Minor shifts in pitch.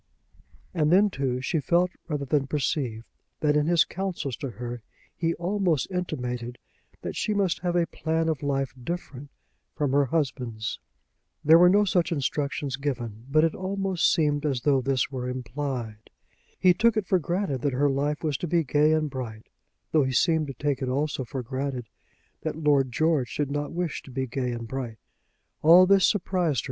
No: average, 4.5 semitones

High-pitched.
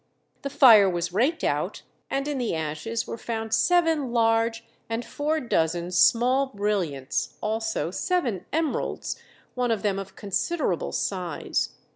Yes: high, 225 Hz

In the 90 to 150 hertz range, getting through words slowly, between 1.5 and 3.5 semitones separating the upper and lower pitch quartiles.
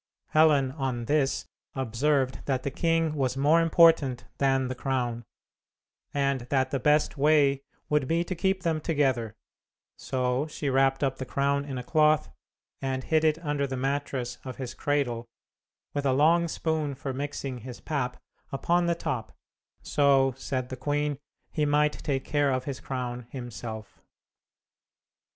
No: medium, 140 Hz; average, 155 wpm; narrow, 2.6 semitones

